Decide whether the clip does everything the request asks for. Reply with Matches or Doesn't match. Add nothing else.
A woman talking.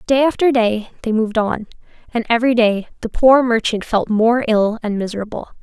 Matches